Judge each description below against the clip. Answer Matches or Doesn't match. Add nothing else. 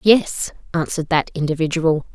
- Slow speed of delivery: Matches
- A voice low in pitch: Doesn't match